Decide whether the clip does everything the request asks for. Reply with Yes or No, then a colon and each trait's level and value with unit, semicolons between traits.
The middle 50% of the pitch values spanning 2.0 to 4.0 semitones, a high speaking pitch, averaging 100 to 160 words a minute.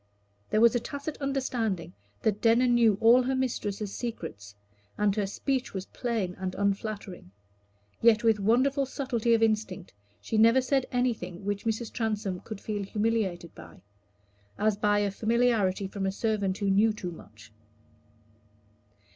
Yes: average, 3.2 semitones; high, 215 Hz; average, 145 wpm